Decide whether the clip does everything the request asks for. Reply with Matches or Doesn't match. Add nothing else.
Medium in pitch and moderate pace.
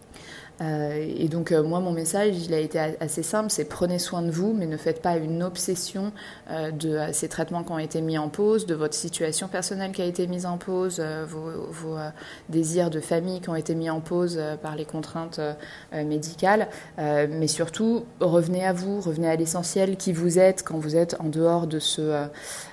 Matches